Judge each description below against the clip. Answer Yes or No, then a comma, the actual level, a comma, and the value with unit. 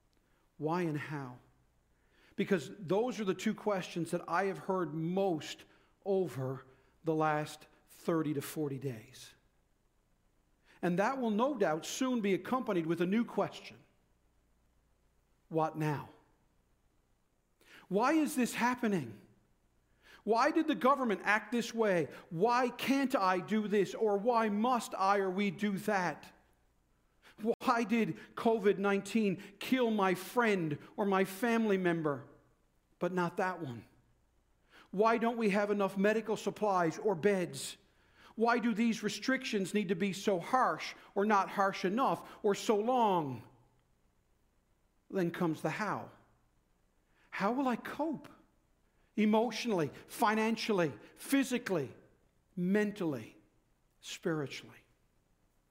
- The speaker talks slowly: Yes, slow, 120 wpm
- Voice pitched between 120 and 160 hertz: No, high, 195 Hz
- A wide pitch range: Yes, wide, 6.1 semitones